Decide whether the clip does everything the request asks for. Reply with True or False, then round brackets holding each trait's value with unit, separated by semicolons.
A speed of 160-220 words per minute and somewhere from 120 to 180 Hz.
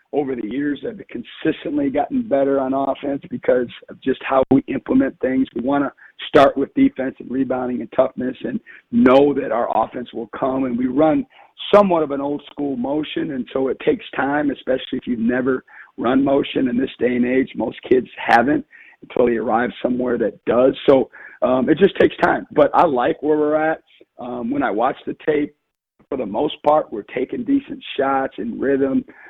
True (195 wpm; 140 Hz)